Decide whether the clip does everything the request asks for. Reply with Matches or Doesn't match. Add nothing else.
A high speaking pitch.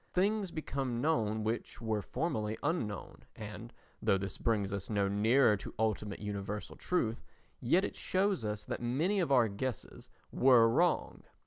Doesn't match